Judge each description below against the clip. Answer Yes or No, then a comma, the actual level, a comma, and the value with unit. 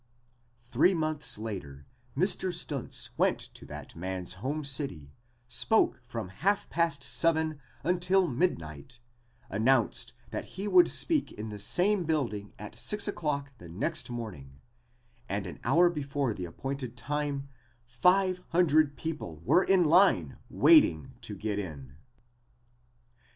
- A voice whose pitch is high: No, low, 135 Hz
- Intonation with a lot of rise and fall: Yes, wide, 8.5 semitones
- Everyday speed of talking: No, slow, 130 wpm